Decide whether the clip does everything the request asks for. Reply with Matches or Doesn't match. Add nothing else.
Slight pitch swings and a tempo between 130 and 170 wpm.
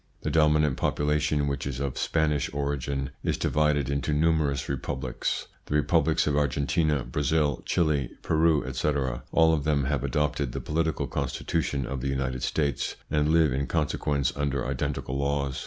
Matches